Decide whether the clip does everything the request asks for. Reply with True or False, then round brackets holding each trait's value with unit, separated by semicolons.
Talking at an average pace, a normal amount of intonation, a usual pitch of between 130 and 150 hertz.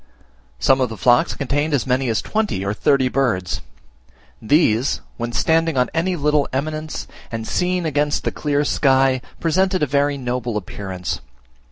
True (155 wpm; 4.1 semitones; 135 Hz)